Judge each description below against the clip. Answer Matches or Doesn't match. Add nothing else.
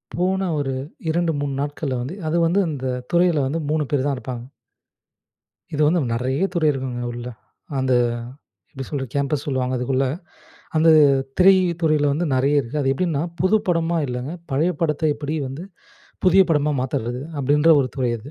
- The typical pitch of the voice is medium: Matches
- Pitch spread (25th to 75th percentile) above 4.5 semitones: Doesn't match